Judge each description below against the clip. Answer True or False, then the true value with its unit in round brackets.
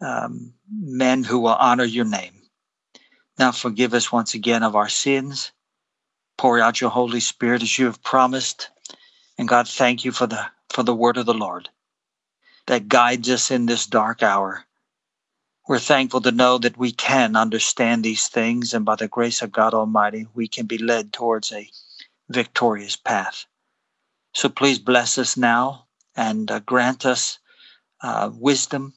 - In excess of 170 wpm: False (165 wpm)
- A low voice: True (120 Hz)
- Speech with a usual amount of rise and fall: False (2.1 semitones)